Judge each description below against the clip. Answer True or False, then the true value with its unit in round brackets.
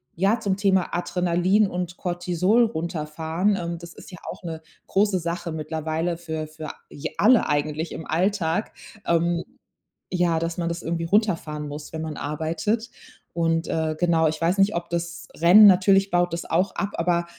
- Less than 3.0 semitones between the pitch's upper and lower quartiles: True (2.6 semitones)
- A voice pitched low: False (170 Hz)